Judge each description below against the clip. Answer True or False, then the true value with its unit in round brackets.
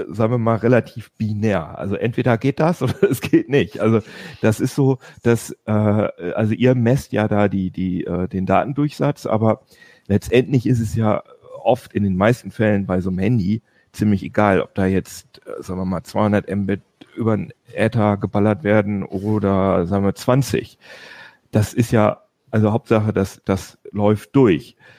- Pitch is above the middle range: False (105 Hz)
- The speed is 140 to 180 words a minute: True (175 wpm)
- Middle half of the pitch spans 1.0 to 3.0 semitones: False (3.7 semitones)